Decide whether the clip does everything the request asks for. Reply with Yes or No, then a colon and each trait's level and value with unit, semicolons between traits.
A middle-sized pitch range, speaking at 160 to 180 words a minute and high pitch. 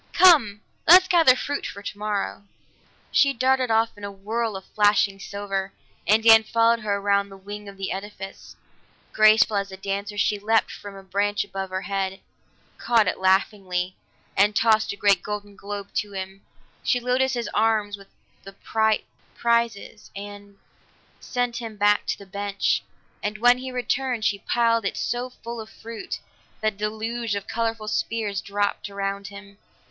No: narrow, 2.3 semitones; average, 165 wpm; high, 205 Hz